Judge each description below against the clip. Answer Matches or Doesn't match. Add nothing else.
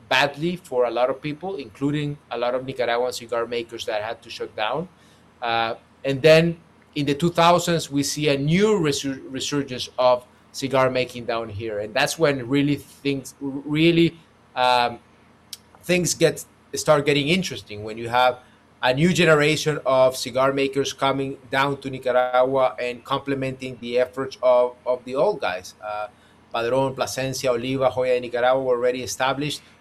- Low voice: Matches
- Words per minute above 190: Doesn't match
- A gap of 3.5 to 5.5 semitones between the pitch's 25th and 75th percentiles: Doesn't match